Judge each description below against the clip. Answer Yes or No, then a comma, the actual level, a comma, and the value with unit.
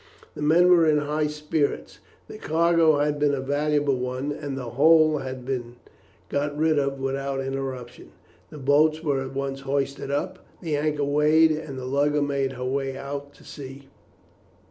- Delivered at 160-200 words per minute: Yes, average, 170 wpm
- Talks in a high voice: No, medium, 145 Hz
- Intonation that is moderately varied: No, narrow, 2.0 semitones